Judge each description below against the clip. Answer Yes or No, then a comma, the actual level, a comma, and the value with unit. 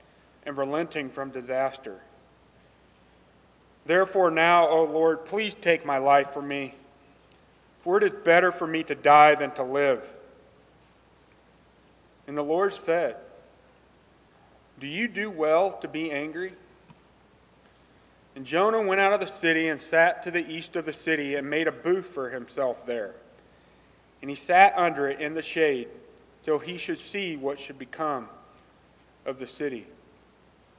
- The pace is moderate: Yes, average, 150 wpm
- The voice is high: No, medium, 160 Hz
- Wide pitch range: No, average, 4.4 semitones